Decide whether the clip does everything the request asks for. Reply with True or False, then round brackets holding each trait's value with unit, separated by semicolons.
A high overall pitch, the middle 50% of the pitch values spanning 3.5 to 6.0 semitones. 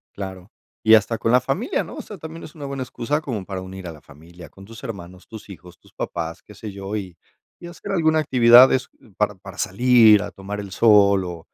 False (105 Hz; 5.1 semitones)